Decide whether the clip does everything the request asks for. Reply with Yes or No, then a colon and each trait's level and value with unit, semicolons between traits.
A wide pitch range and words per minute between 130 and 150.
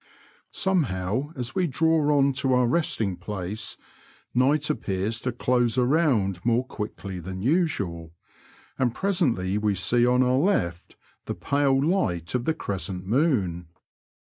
Yes: wide, 7.0 semitones; average, 140 wpm